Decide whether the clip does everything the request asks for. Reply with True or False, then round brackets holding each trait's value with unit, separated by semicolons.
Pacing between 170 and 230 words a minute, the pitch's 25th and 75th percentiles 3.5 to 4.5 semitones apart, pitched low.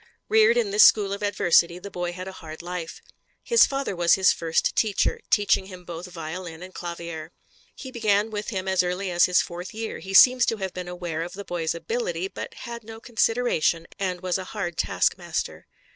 False (200 wpm; 4.2 semitones; 185 Hz)